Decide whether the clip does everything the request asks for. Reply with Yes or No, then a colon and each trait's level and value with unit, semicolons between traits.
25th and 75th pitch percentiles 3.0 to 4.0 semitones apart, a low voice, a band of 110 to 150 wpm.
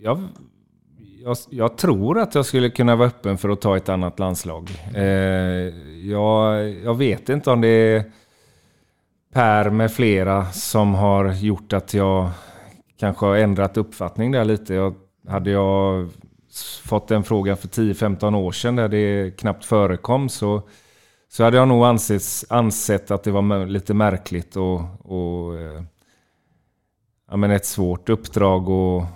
No: narrow, 2.5 semitones; low, 100 Hz; average, 145 wpm